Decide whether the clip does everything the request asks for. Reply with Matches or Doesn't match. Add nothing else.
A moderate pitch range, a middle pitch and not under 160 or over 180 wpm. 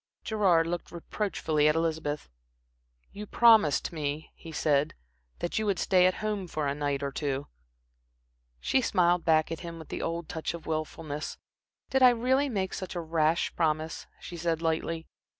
Matches